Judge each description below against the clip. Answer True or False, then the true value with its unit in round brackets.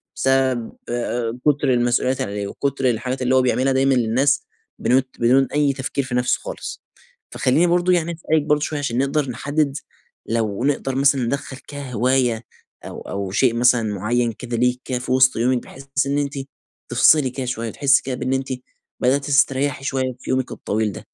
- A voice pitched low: True (130 Hz)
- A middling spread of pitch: False (2.2 semitones)